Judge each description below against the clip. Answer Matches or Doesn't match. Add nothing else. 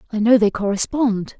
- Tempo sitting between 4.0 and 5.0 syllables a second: Doesn't match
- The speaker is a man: Doesn't match